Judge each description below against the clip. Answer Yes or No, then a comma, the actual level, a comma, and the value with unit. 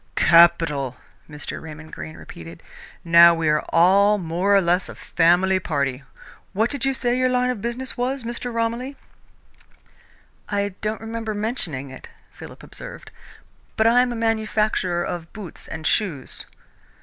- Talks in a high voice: Yes, high, 200 Hz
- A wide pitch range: Yes, wide, 5.7 semitones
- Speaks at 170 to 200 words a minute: No, average, 150 wpm